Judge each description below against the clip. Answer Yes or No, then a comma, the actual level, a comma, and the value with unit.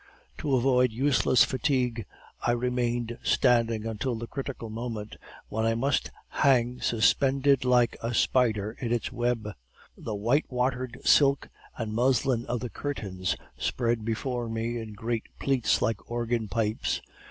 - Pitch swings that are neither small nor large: No, narrow, 2.2 semitones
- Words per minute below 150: Yes, average, 140 wpm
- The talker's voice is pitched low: Yes, low, 120 Hz